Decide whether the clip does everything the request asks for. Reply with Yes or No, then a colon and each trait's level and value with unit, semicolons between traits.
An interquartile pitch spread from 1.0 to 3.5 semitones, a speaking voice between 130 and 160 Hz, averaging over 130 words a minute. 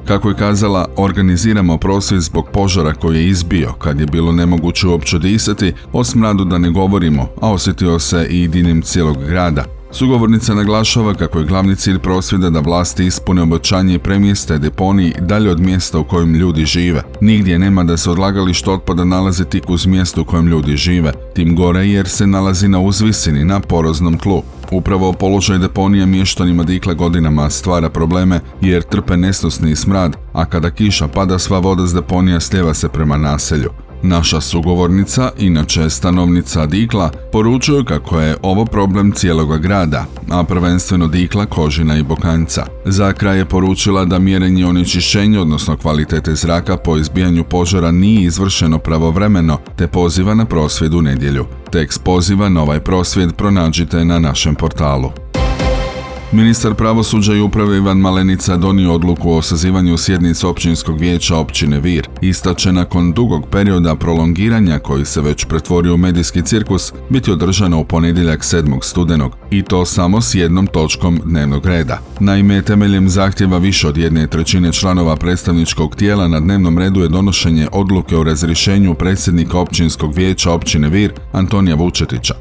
No: average, 2.8 semitones; very low, 90 Hz; average, 155 wpm